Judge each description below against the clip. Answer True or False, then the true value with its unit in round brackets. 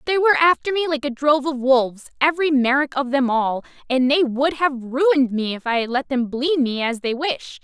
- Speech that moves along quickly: True (220 wpm)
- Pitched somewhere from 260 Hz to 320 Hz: True (275 Hz)